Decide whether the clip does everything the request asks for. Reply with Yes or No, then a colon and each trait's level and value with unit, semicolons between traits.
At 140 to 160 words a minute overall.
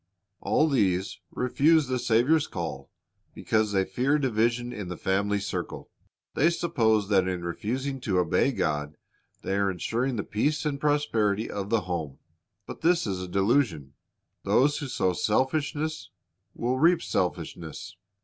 Yes: average, 145 wpm